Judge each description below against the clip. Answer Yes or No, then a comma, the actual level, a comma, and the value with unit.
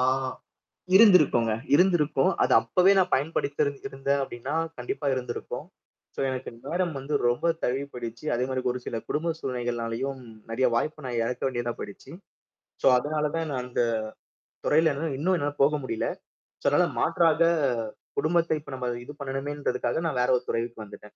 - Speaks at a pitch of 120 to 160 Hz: Yes, low, 135 Hz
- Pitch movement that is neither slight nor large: Yes, average, 4.0 semitones